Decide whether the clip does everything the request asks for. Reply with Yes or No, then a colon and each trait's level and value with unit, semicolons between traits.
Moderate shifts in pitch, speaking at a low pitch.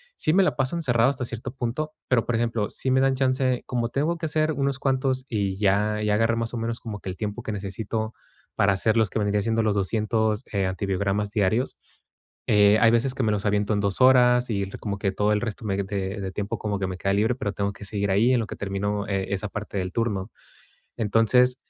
Yes: average, 3.4 semitones; low, 110 Hz